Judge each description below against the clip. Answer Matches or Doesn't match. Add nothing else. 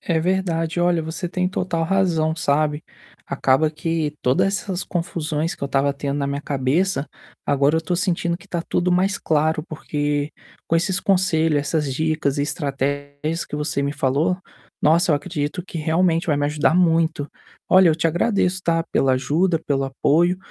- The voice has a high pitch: Doesn't match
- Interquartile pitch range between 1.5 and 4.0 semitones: Matches